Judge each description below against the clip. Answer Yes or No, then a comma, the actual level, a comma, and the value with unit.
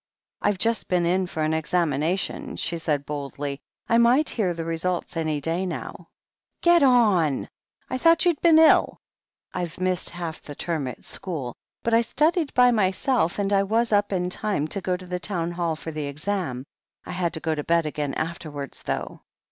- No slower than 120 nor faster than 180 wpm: No, average, 190 wpm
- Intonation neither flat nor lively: Yes, average, 4.9 semitones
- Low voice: No, medium, 175 Hz